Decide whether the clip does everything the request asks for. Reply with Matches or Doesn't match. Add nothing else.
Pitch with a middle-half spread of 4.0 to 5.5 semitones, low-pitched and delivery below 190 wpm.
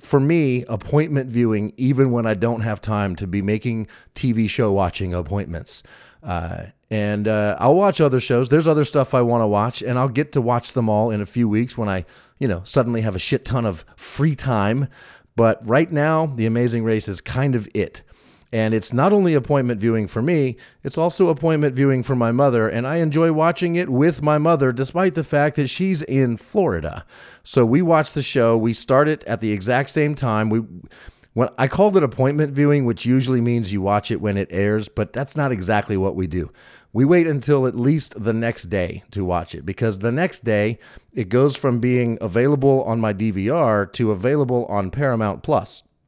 Doesn't match